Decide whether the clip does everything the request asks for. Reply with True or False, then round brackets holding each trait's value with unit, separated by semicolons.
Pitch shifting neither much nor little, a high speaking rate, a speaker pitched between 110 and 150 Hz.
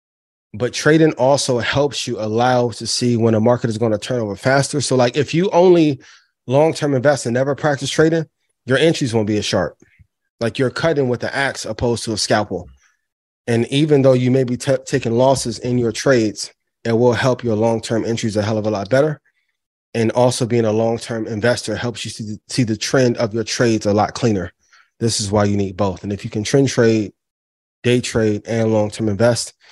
True (3.4 semitones; 220 wpm; 120 Hz)